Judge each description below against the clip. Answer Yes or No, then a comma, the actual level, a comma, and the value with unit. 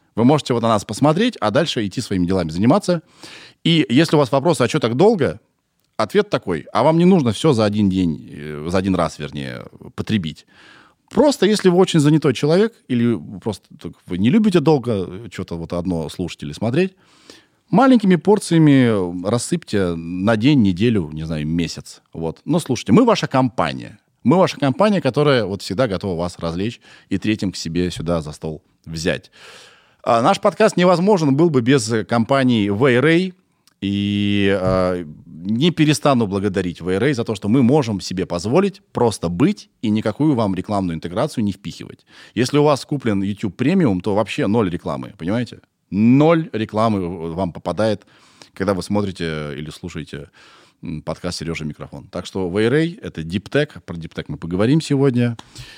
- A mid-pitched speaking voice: No, low, 110 Hz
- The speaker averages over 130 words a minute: Yes, fast, 160 wpm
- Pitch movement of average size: No, wide, 8.8 semitones